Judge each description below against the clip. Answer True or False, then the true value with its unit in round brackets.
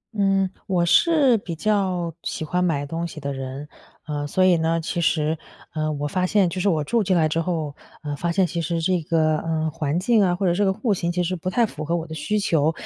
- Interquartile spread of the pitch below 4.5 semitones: True (3.1 semitones)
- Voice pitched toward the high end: False (170 Hz)